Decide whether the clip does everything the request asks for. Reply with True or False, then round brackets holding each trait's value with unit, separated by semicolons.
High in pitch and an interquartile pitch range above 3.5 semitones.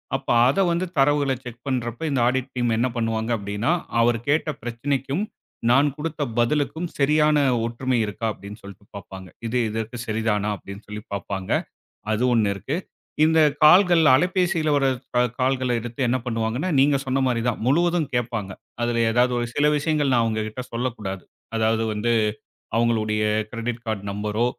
False (120 Hz; 4.2 semitones)